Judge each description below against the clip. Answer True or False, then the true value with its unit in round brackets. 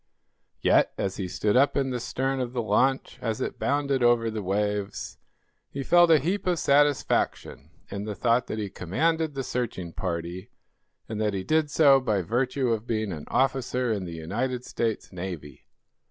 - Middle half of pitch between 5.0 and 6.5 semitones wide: True (5.3 semitones)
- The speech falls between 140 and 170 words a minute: False (180 wpm)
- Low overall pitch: True (120 Hz)